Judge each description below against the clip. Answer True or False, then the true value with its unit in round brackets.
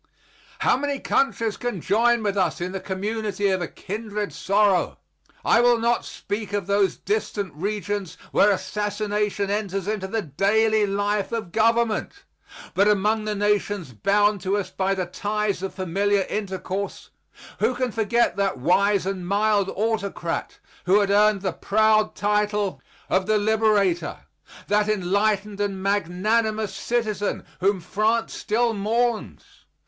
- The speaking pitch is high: True (205 Hz)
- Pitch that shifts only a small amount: True (1.8 semitones)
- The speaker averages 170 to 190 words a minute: False (140 wpm)